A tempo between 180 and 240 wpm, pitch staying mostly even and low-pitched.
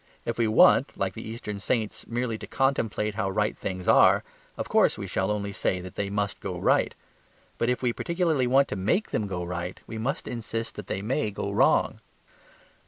No: average, 200 wpm; average, 3.5 semitones; low, 110 Hz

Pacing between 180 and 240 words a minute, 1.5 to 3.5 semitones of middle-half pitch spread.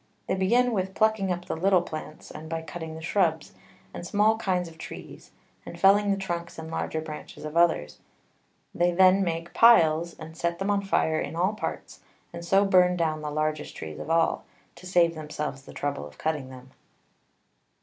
Yes: average, 190 wpm; average, 3.2 semitones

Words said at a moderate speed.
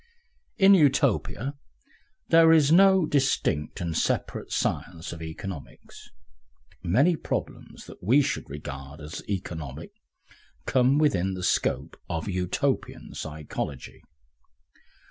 No: slow, 105 wpm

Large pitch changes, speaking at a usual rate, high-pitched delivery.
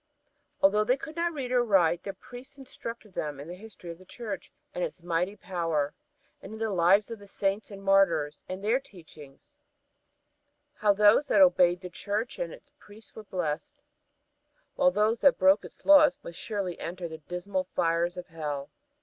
No: average, 4.6 semitones; average, 185 wpm; high, 195 Hz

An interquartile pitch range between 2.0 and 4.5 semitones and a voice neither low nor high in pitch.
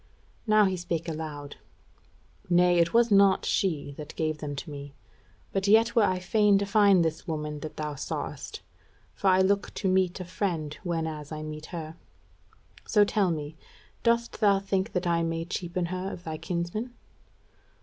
Yes: average, 4.0 semitones; medium, 175 Hz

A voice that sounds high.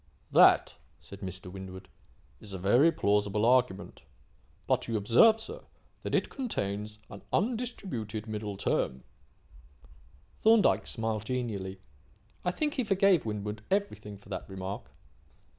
No: low, 110 Hz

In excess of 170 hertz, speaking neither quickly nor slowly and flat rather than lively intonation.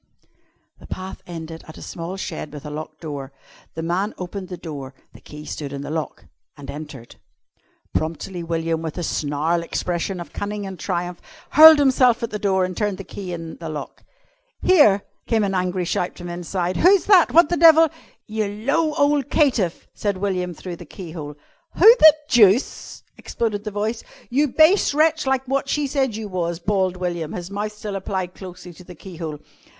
No: medium, 185 Hz; average, 190 wpm; average, 5.2 semitones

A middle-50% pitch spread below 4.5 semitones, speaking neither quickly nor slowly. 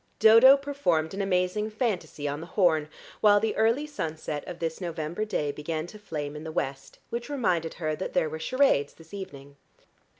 No: wide, 5.6 semitones; average, 185 wpm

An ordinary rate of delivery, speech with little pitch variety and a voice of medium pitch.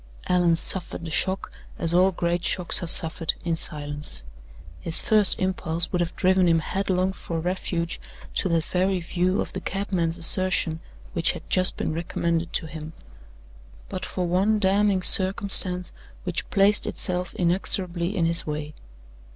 Yes: average, 150 wpm; narrow, 2.1 semitones; medium, 180 Hz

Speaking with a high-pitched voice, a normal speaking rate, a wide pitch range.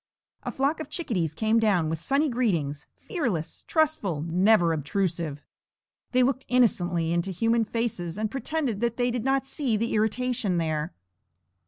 Yes: high, 220 Hz; average, 150 wpm; wide, 6.8 semitones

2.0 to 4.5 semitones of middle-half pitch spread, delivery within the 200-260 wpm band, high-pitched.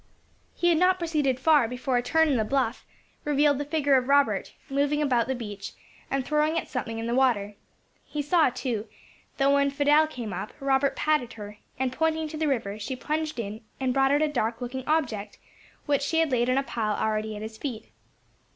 Yes: average, 4.2 semitones; fast, 205 wpm; very high, 270 Hz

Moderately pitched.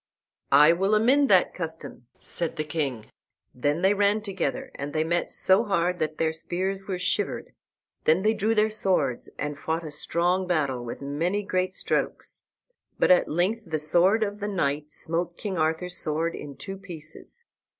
Yes: medium, 175 Hz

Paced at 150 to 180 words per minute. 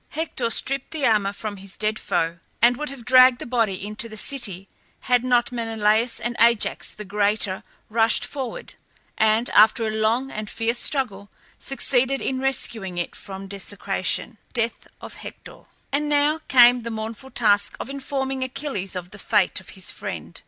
Yes: average, 165 wpm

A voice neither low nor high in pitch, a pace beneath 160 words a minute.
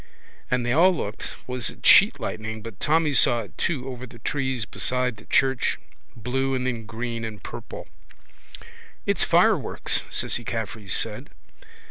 No: low, 120 Hz; average, 150 wpm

